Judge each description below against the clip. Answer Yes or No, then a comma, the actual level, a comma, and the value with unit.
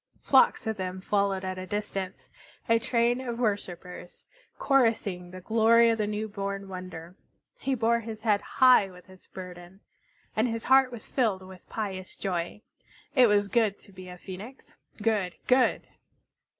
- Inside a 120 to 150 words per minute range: No, average, 160 wpm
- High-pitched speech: Yes, high, 205 Hz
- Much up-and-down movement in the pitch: No, average, 3.7 semitones